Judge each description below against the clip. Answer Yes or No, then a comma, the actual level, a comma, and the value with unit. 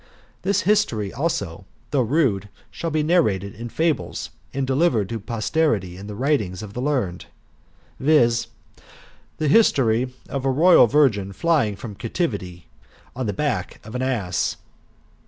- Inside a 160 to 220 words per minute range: No, average, 140 wpm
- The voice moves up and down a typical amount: No, wide, 6.7 semitones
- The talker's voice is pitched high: No, low, 120 Hz